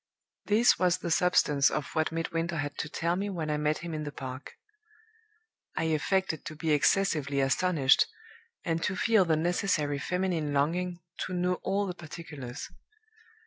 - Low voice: No, medium, 165 Hz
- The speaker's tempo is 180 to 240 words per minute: No, average, 160 wpm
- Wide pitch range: No, average, 3.4 semitones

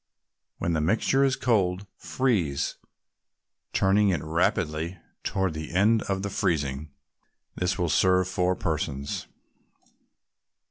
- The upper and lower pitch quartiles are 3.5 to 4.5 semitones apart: Yes, average, 4.0 semitones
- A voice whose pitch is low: Yes, very low, 90 Hz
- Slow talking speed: Yes, slow, 110 wpm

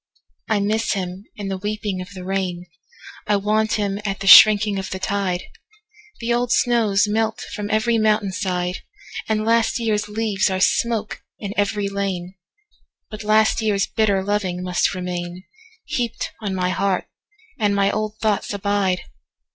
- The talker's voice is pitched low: No, high, 205 Hz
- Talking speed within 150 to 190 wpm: No, average, 140 wpm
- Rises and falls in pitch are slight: Yes, narrow, 2.3 semitones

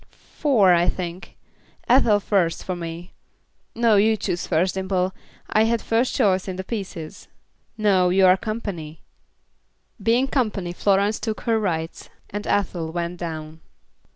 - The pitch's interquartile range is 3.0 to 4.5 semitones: Yes, average, 3.7 semitones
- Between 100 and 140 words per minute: Yes, slow, 135 wpm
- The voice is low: No, high, 190 Hz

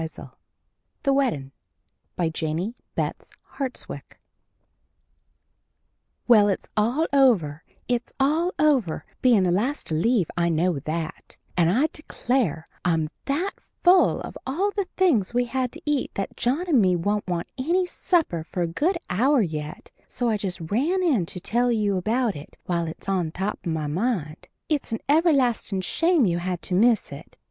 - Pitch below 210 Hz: No, high, 215 Hz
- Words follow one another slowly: No, average, 160 wpm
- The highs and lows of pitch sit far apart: Yes, wide, 8.1 semitones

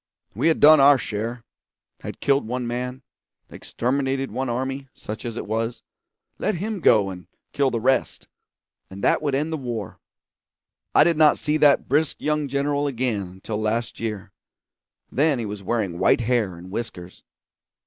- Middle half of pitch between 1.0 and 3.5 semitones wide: No, average, 4.5 semitones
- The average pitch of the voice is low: Yes, low, 125 Hz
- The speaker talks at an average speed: Yes, average, 165 wpm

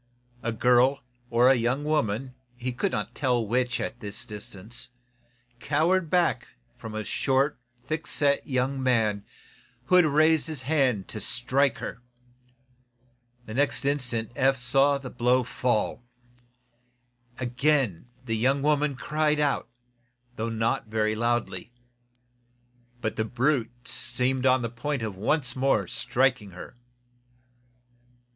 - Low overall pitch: Yes, low, 125 Hz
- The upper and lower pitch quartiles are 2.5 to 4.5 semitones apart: Yes, average, 3.4 semitones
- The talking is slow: Yes, slow, 125 wpm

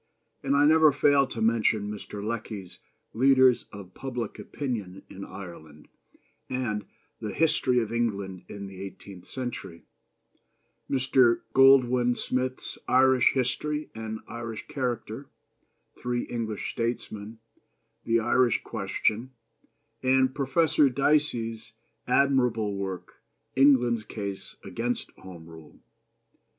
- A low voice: Yes, low, 120 Hz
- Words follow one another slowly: Yes, slow, 105 wpm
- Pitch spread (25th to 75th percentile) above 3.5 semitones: Yes, average, 4.0 semitones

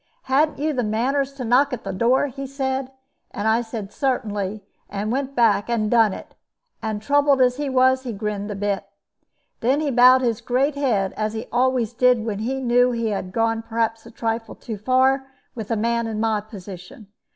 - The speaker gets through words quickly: No, average, 195 wpm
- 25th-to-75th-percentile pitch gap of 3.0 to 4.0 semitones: Yes, average, 3.4 semitones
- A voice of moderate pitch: No, high, 235 Hz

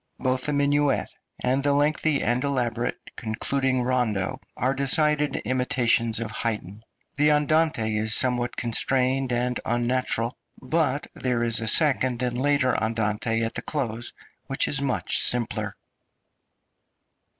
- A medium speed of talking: No, slow, 130 wpm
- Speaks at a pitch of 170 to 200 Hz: No, low, 125 Hz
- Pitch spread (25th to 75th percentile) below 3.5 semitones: Yes, average, 3.1 semitones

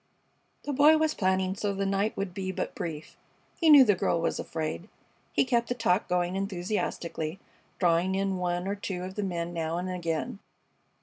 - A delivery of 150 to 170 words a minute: No, average, 185 wpm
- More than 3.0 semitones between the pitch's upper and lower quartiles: No, average, 2.7 semitones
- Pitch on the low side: No, high, 190 Hz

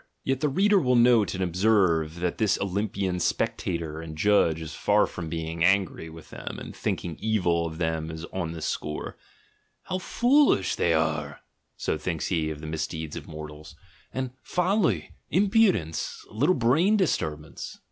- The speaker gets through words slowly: No, average, 160 wpm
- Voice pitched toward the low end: Yes, very low, 90 Hz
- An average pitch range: No, wide, 7.1 semitones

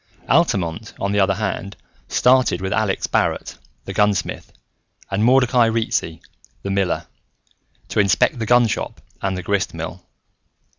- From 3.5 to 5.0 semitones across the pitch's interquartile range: No, average, 3.1 semitones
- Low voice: Yes, low, 100 Hz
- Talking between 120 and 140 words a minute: Yes, slow, 135 wpm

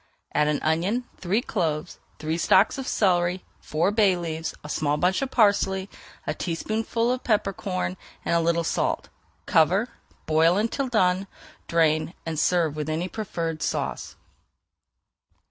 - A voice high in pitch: No, medium, 180 Hz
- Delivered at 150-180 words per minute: No, average, 140 wpm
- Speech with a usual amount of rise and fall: Yes, average, 4.2 semitones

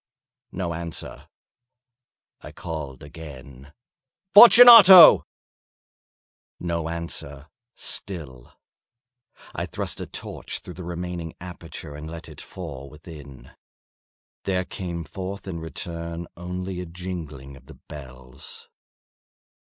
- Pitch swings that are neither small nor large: Yes, average, 3.6 semitones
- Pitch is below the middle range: Yes, very low, 85 Hz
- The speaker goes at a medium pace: No, slow, 100 wpm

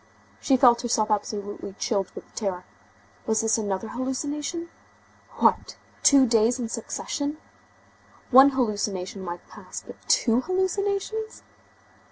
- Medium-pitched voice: No, high, 235 Hz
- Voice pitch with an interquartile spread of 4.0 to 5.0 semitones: No, wide, 5.4 semitones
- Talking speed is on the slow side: Yes, slow, 115 wpm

